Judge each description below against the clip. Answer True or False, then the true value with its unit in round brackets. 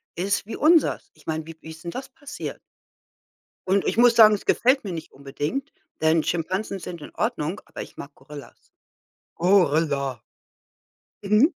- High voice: False (180 Hz)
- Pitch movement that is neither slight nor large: False (6.4 semitones)